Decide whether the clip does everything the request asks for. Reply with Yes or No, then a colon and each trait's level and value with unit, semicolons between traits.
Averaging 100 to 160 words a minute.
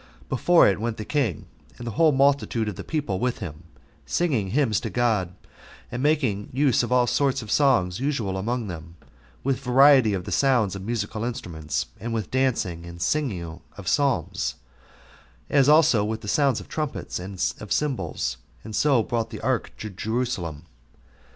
No: average, 170 wpm